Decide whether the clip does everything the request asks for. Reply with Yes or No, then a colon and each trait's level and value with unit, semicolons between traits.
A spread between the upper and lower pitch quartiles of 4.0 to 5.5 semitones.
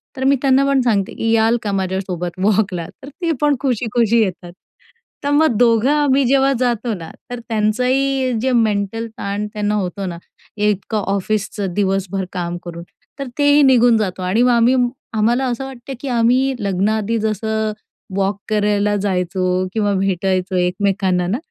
Yes: average, 4.3 semitones